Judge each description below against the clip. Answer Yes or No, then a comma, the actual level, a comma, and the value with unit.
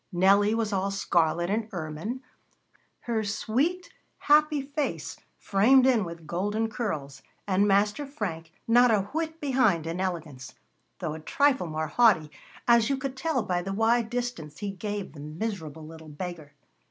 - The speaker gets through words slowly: No, average, 155 wpm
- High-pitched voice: Yes, high, 205 Hz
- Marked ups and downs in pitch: Yes, wide, 6.5 semitones